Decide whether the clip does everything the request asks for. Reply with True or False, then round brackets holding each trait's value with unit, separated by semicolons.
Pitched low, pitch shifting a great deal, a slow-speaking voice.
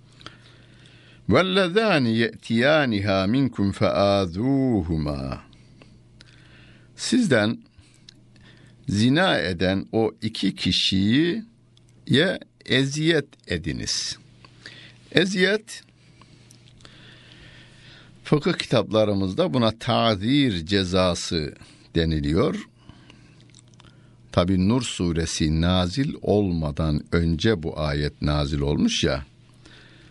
True (105 Hz; 5.7 semitones; 60 wpm)